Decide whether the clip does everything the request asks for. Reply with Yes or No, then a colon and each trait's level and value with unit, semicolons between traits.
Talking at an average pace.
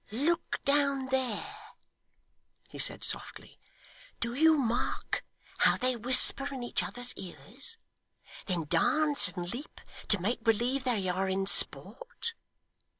No: slow, 125 wpm